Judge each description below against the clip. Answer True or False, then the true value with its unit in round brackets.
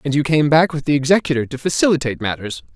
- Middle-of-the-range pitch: True (145 Hz)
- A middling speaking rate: False (220 wpm)